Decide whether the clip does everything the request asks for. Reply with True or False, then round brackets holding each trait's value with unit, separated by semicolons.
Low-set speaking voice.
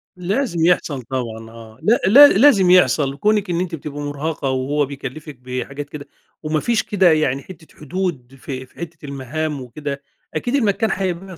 False (155 Hz)